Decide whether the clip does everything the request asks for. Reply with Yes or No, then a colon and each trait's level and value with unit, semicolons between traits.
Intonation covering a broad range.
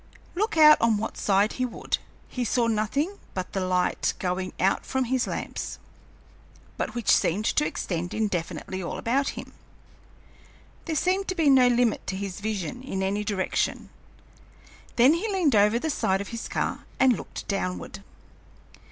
Yes: wide, 5.9 semitones